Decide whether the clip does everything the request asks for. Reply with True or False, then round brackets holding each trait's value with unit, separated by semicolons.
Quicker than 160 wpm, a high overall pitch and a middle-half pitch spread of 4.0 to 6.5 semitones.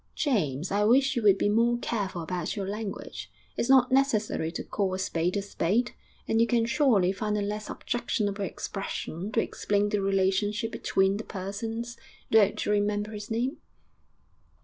False (170 wpm; 205 Hz; 2.9 semitones)